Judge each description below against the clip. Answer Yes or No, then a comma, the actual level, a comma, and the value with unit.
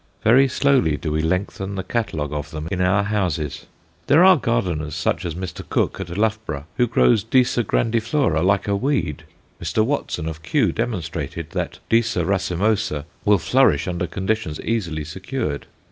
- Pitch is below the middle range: Yes, very low, 95 Hz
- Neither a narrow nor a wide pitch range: No, wide, 6.1 semitones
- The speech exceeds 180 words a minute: No, average, 160 wpm